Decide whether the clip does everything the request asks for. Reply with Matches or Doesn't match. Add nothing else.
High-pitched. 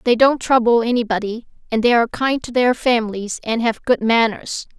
Matches